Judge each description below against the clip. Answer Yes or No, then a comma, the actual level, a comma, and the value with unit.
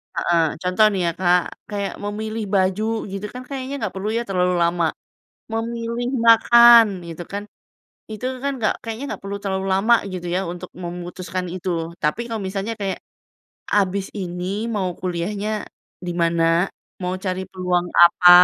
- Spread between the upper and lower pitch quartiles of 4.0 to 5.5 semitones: No, average, 3.3 semitones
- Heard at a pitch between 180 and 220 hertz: Yes, high, 190 Hz